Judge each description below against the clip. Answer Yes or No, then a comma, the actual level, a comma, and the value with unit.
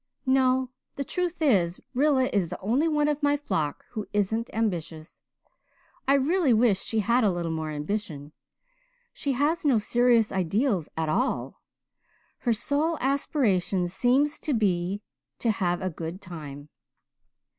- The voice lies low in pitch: No, high, 225 Hz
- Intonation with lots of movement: Yes, wide, 7.5 semitones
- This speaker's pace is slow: No, average, 145 wpm